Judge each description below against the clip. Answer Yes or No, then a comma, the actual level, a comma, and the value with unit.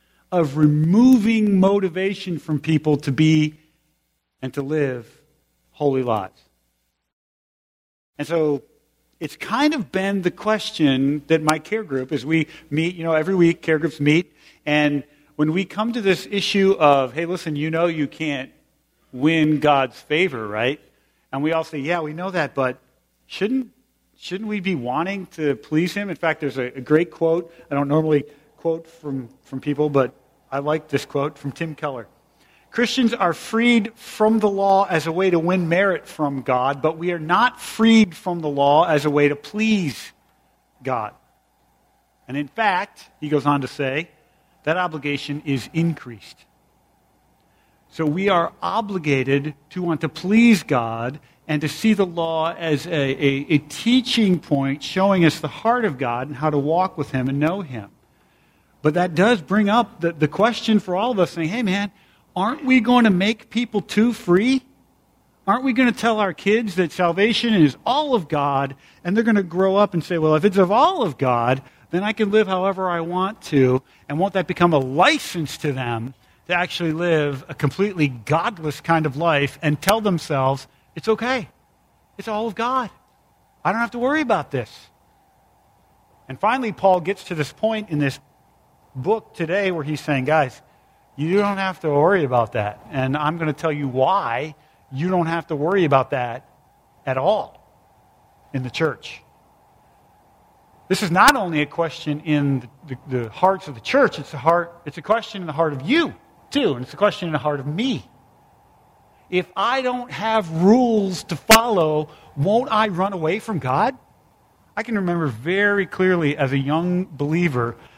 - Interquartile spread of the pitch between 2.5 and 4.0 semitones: No, average, 5.3 semitones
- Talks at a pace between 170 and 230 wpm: Yes, average, 180 wpm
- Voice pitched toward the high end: No, medium, 160 Hz